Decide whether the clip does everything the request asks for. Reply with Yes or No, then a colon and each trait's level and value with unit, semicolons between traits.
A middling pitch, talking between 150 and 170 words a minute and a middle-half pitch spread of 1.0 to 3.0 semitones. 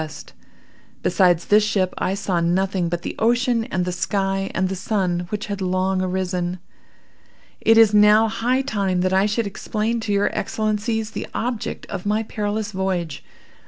No: high, 200 Hz; average, 165 wpm; narrow, 2.6 semitones